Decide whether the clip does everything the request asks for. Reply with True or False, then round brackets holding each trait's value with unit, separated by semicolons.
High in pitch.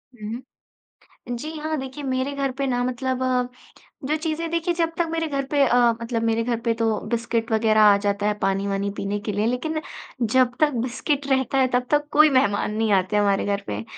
True (245 Hz)